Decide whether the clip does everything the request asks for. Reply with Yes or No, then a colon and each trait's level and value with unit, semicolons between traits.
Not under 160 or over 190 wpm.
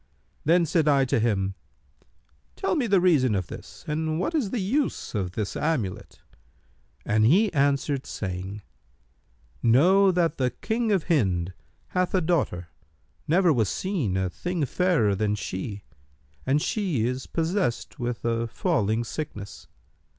No: average, 145 wpm